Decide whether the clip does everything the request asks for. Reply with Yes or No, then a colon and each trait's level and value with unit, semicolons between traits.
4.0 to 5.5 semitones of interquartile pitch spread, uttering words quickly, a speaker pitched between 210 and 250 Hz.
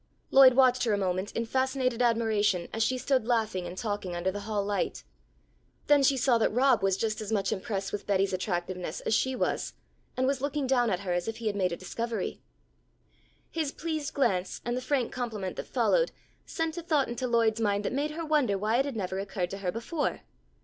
Yes: average, 4.9 semitones; fast, 210 wpm; high, 225 Hz